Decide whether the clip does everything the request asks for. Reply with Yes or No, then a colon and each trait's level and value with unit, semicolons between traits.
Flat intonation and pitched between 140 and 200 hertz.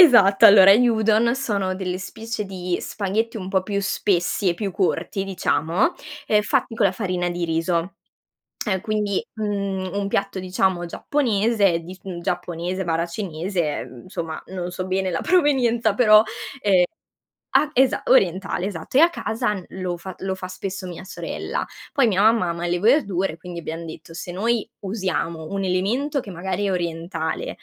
No: average, 3.2 semitones; high, 190 Hz